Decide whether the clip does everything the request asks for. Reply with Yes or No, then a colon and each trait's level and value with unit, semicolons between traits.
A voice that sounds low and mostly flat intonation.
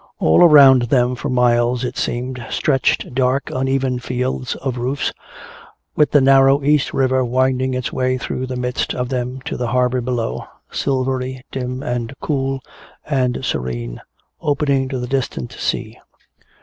Yes: low, 130 Hz; narrow, 1.3 semitones